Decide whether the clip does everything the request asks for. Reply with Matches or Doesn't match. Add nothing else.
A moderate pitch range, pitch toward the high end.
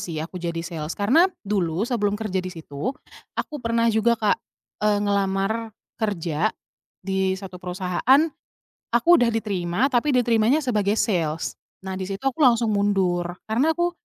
Matches